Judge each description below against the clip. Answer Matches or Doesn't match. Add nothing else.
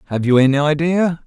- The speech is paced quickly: Doesn't match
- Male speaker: Matches